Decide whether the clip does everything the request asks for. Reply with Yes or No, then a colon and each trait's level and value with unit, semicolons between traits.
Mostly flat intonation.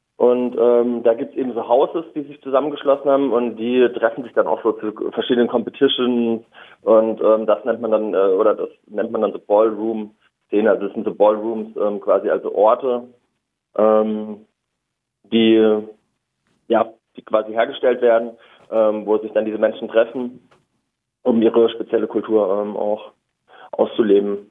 Yes: narrow, 2.3 semitones